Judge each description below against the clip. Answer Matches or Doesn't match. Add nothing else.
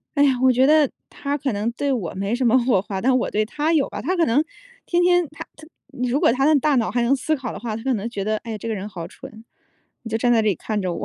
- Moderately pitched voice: Doesn't match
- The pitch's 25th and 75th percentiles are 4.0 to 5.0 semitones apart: Matches